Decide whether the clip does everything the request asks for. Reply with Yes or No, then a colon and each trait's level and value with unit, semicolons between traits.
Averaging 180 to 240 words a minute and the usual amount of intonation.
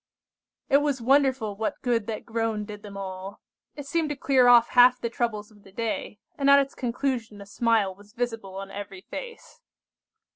Yes: average, 185 wpm; average, 4.1 semitones